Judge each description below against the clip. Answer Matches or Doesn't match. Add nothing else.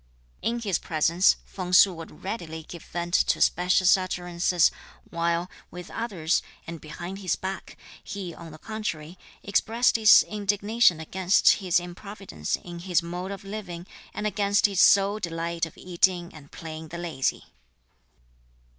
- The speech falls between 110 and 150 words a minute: Matches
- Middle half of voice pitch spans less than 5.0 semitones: Matches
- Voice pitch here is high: Doesn't match